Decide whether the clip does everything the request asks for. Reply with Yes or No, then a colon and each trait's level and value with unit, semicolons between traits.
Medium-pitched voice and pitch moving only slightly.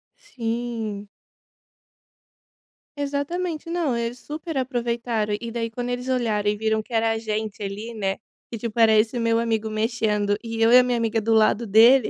No: high, 230 Hz; narrow, 2.1 semitones